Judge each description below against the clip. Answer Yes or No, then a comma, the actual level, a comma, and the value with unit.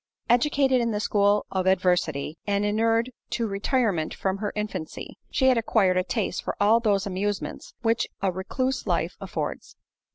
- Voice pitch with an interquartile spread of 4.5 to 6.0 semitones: No, average, 3.4 semitones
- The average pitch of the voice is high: Yes, high, 205 Hz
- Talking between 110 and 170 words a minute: Yes, average, 160 wpm